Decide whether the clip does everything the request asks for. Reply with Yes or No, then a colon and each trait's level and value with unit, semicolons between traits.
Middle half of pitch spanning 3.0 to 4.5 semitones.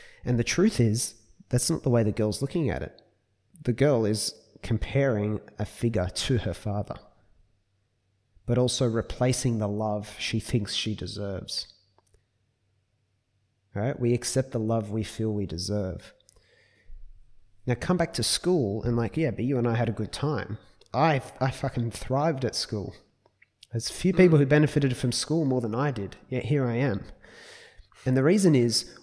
Yes: average, 3.9 semitones